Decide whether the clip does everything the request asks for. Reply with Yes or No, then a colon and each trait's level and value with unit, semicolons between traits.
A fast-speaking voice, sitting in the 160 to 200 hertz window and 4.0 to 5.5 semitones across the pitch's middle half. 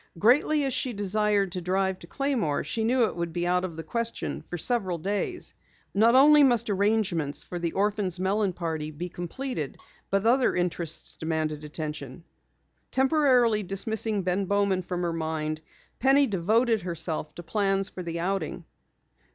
No: average, 160 wpm; high, 190 Hz; average, 4.9 semitones